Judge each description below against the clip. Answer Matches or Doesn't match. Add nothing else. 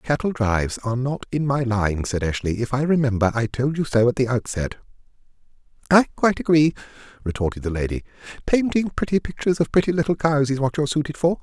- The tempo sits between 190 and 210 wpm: Matches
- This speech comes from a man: Matches